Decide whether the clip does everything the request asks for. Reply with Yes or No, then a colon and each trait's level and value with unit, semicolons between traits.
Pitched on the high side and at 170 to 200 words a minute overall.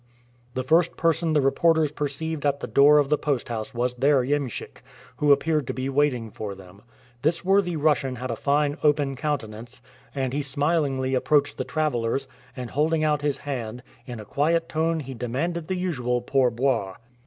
No: medium, 140 Hz; average, 180 wpm